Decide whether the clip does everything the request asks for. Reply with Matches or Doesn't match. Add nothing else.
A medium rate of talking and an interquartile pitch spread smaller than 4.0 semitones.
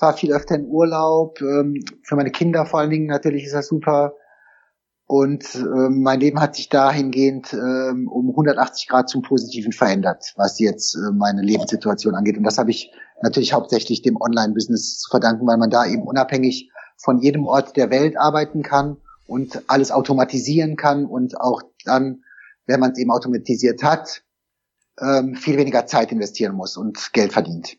Matches